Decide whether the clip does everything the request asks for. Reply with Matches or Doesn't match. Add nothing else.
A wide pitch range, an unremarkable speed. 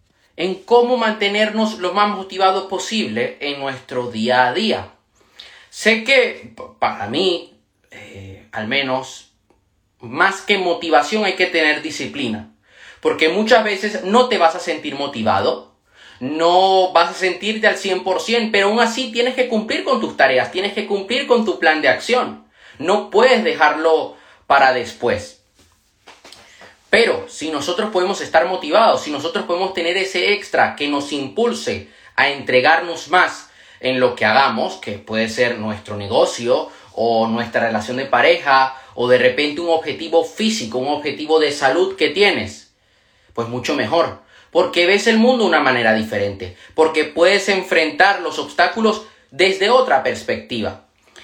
Matches